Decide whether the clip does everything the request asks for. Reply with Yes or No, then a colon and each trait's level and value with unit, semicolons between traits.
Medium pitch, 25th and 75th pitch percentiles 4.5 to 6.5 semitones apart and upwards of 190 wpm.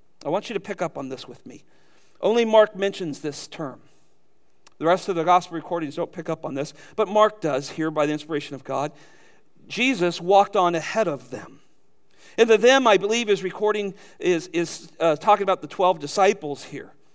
Yes: medium, 175 Hz; average, 5.1 semitones; average, 200 wpm